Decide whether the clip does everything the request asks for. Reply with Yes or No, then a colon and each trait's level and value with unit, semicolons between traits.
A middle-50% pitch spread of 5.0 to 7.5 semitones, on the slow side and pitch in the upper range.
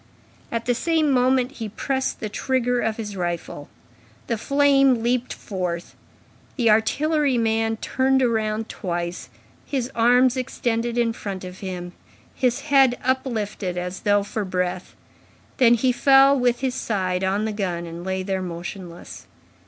No: average, 5.3 semitones; average, 145 wpm; high, 225 Hz